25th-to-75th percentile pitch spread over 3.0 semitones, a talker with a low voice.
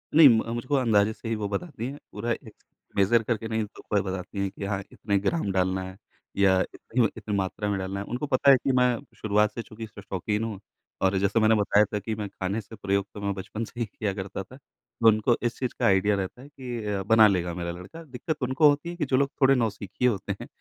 Yes: average, 3.5 semitones; low, 105 Hz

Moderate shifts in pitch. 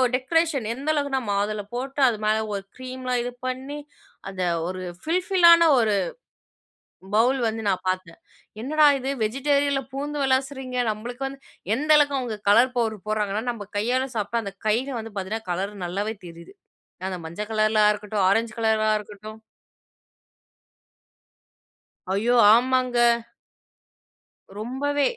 Yes: average, 4.2 semitones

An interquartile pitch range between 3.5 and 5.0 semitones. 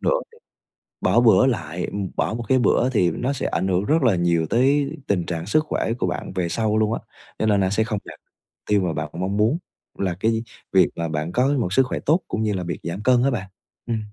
No: wide, 5.6 semitones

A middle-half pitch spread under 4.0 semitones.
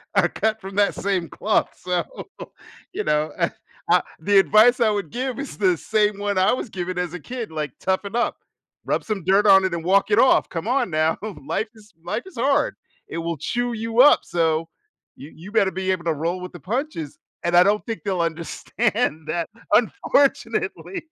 No: average, 4.7 semitones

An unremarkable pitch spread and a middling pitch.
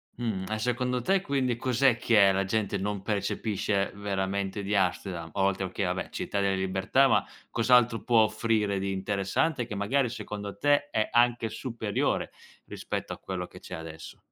No: average, 3.6 semitones; low, 105 Hz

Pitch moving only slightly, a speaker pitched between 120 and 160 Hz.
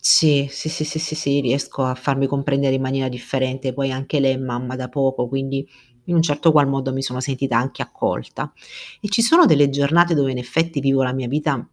Yes: narrow, 1.9 semitones; low, 135 Hz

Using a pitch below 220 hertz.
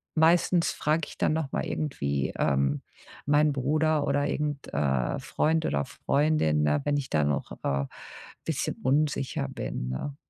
Yes: medium, 140 Hz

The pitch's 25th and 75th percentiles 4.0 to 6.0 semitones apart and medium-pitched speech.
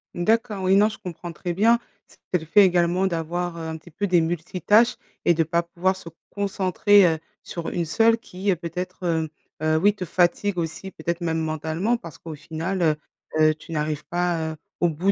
No: average, 2.9 semitones; medium, 175 Hz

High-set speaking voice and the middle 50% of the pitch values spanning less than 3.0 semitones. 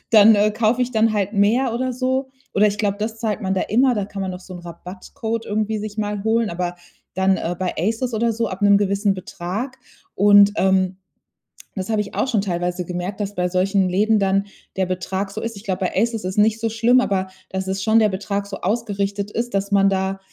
Yes: high, 205 Hz; narrow, 2.6 semitones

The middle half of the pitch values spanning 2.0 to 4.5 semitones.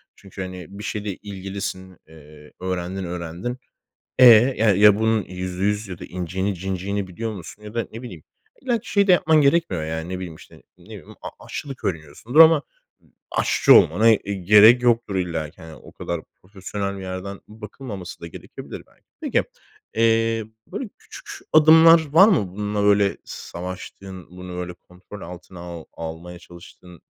Yes: average, 4.1 semitones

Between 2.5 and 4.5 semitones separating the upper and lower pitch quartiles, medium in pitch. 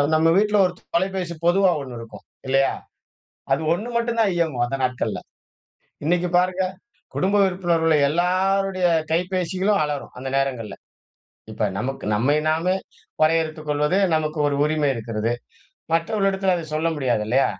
No: average, 5.3 semitones; medium, 165 Hz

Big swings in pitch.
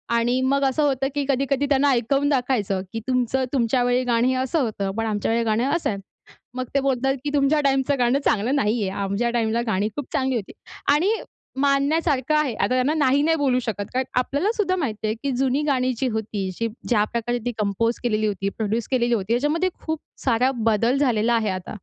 No: average, 3.7 semitones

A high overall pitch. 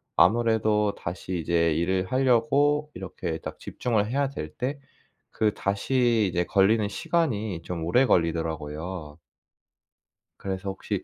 No: low, 100 Hz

